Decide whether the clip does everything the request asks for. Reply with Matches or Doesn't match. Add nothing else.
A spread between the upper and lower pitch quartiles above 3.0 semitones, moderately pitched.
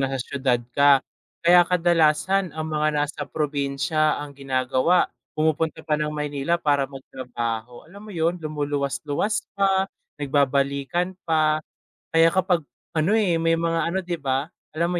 Matches